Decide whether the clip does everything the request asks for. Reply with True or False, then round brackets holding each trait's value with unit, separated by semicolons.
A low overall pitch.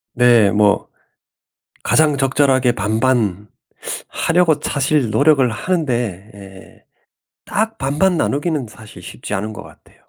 True (125 Hz)